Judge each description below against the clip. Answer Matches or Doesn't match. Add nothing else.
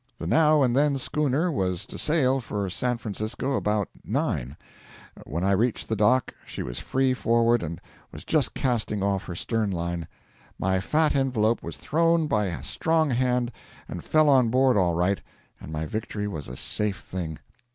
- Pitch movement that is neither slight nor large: Doesn't match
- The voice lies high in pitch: Doesn't match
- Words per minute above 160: Matches